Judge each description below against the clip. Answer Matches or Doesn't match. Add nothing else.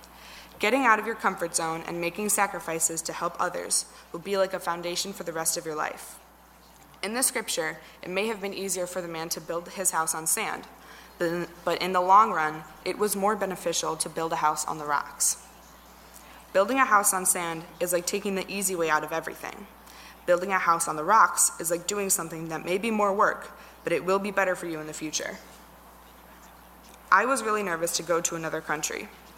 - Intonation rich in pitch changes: Doesn't match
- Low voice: Doesn't match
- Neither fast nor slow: Doesn't match